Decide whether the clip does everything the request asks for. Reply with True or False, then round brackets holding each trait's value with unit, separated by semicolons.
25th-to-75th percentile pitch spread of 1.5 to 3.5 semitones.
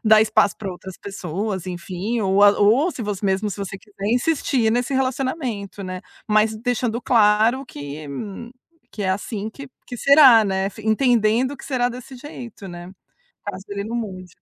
False (4.0 semitones)